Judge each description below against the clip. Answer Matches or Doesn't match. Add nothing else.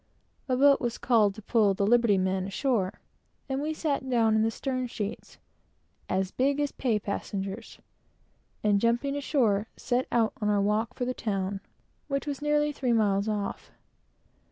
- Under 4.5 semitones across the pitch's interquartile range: Doesn't match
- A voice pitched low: Doesn't match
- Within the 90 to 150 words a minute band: Doesn't match